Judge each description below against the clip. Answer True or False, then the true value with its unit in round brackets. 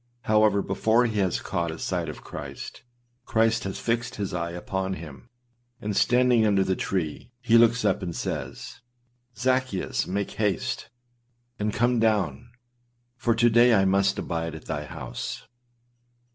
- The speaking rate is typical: True (150 wpm)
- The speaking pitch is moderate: False (105 Hz)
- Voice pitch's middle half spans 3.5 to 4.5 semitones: True (4.1 semitones)